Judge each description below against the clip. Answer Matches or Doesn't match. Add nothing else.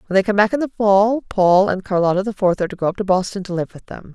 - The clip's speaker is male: Doesn't match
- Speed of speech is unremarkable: Doesn't match